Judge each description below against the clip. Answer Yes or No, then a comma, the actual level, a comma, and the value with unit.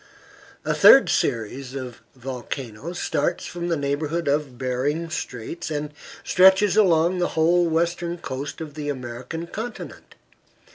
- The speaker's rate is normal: No, slow, 130 wpm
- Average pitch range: Yes, average, 4.5 semitones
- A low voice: No, medium, 150 Hz